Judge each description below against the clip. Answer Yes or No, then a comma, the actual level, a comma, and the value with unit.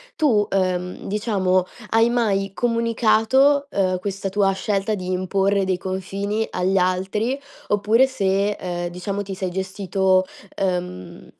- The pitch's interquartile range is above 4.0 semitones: No, narrow, 2.5 semitones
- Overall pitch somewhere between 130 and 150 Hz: No, high, 195 Hz